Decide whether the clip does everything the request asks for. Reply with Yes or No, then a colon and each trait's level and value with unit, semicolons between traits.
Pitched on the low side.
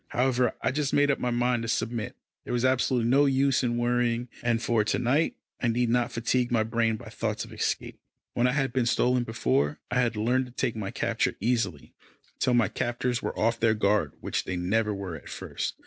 Yes: low, 120 Hz